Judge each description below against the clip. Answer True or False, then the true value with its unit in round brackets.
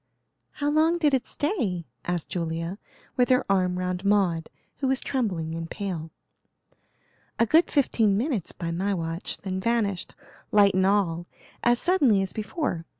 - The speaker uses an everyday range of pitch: False (6.2 semitones)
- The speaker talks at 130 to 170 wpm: True (150 wpm)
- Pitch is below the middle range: False (200 Hz)